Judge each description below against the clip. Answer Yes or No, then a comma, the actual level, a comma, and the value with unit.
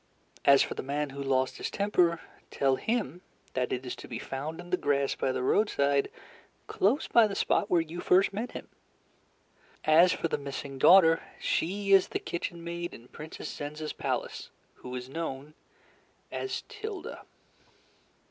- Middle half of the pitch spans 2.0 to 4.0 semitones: No, average, 4.8 semitones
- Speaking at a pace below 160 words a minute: No, average, 165 wpm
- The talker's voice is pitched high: No, medium, 160 Hz